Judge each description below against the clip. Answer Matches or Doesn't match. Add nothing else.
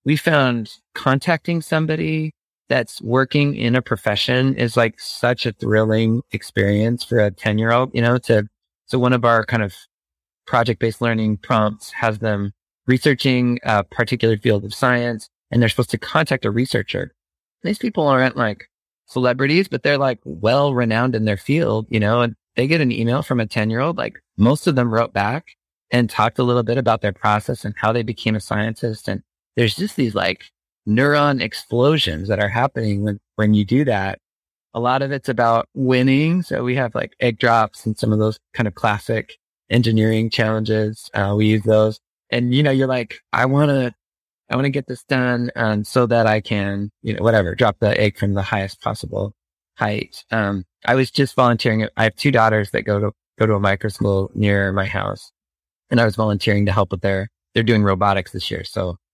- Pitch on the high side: Doesn't match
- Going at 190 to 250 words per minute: Matches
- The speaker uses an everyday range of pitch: Matches